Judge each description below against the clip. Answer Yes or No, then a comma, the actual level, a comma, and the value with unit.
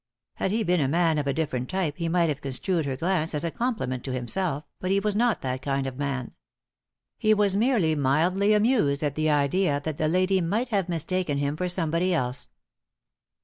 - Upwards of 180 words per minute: Yes, fast, 205 wpm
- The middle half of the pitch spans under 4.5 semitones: No, average, 5.1 semitones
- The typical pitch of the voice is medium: Yes, medium, 165 Hz